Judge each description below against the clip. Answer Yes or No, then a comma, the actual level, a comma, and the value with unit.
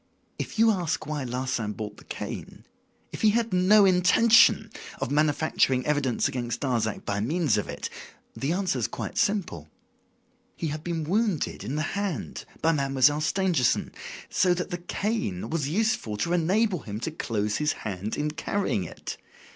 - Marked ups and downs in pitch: Yes, wide, 7.0 semitones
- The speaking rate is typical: Yes, average, 165 wpm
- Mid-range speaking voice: Yes, medium, 150 Hz